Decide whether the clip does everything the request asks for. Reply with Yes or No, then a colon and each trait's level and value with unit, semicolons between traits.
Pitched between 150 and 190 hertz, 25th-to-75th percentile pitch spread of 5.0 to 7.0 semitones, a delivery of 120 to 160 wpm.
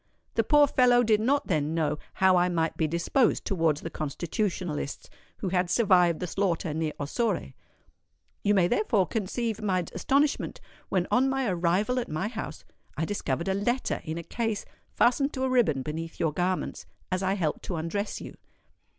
No: medium, 185 Hz; wide, 5.6 semitones; average, 175 wpm